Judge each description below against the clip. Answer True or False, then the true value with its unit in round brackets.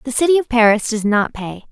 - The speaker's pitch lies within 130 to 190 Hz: False (235 Hz)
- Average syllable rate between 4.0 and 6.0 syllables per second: True (5.8 syllables/s)